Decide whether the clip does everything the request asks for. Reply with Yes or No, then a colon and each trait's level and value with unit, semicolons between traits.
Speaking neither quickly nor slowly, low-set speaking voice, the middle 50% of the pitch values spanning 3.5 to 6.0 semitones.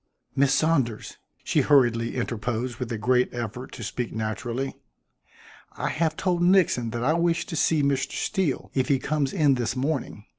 Yes: average, 170 wpm; low, 130 Hz; average, 4.5 semitones